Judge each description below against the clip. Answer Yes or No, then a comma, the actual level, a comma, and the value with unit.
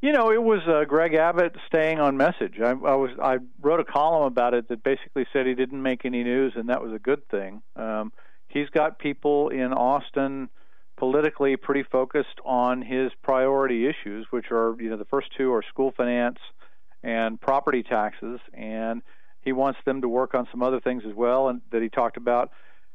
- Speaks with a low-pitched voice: Yes, low, 130 Hz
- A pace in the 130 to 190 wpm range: No, average, 200 wpm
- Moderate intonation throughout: No, narrow, 2.3 semitones